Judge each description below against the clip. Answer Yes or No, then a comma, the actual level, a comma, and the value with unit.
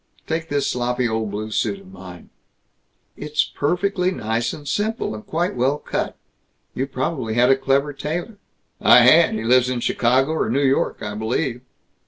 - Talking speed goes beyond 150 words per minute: Yes, average, 175 wpm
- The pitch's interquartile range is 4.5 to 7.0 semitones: Yes, average, 5.2 semitones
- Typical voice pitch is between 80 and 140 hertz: Yes, low, 135 Hz